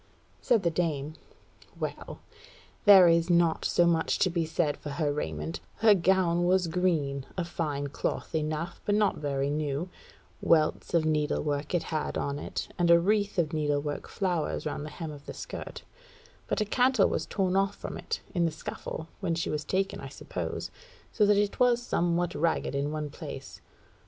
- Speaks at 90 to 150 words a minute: No, average, 185 wpm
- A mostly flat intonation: No, average, 3.7 semitones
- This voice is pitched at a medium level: Yes, medium, 165 Hz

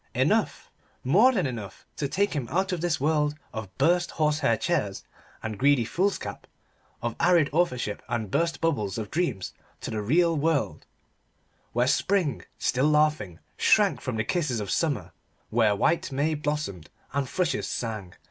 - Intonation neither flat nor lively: No, wide, 6.8 semitones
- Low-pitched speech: No, medium, 145 Hz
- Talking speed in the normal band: Yes, average, 155 wpm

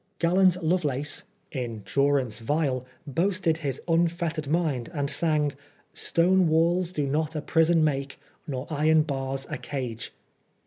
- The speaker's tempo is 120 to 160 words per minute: Yes, average, 145 wpm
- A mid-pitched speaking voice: Yes, medium, 150 Hz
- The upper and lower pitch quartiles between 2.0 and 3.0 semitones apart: No, average, 3.4 semitones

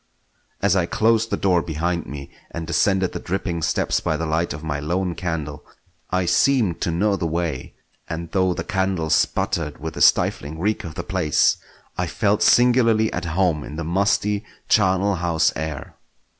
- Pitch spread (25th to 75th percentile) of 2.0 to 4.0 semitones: Yes, average, 3.3 semitones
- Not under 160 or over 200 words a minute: Yes, average, 175 wpm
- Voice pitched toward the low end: Yes, very low, 85 Hz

